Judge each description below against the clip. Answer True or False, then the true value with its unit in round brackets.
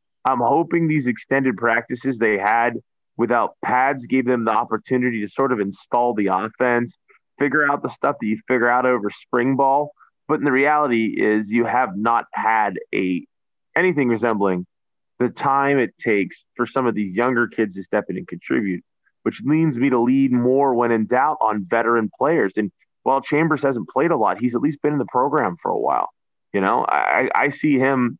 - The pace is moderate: True (195 wpm)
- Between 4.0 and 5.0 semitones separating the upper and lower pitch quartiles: False (3.0 semitones)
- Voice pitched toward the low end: True (125 Hz)